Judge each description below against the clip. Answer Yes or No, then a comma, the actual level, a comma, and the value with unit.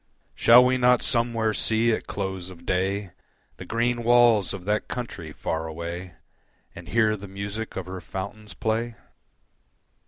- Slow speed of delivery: No, average, 150 wpm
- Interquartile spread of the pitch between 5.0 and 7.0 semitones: No, average, 3.8 semitones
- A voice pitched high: No, low, 105 Hz